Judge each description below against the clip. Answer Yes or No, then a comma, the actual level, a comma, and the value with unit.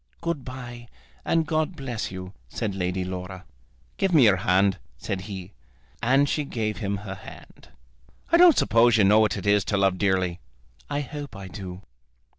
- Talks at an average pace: Yes, average, 175 wpm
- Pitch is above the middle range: No, low, 105 Hz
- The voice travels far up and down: Yes, wide, 5.8 semitones